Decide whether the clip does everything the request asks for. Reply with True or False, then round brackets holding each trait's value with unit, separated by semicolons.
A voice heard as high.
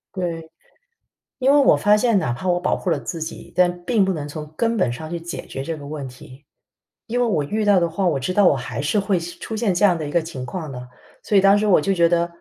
False (175 Hz)